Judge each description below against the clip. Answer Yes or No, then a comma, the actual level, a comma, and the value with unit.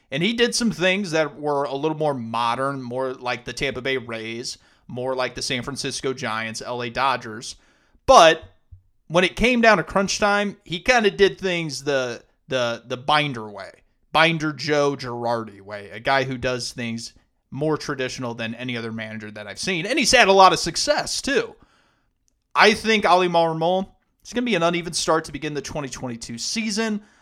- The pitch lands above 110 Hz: Yes, medium, 140 Hz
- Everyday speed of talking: Yes, average, 190 wpm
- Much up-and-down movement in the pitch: Yes, wide, 6.5 semitones